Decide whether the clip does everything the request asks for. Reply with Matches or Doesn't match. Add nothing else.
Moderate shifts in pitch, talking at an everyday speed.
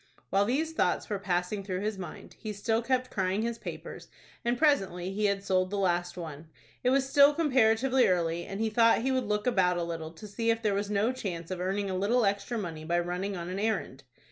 Doesn't match